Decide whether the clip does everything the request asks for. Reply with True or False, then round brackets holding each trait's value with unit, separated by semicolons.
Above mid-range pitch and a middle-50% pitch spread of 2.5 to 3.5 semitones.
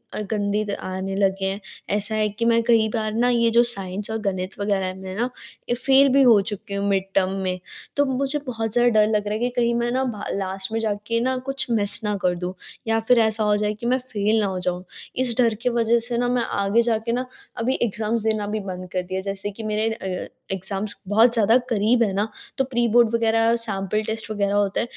True (215 Hz; 2.9 semitones)